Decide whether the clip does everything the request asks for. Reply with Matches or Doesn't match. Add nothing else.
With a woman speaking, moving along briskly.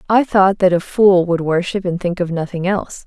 Matches